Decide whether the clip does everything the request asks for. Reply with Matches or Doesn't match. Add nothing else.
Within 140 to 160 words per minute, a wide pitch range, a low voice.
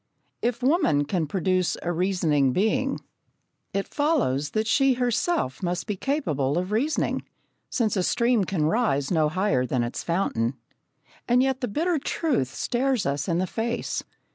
Doesn't match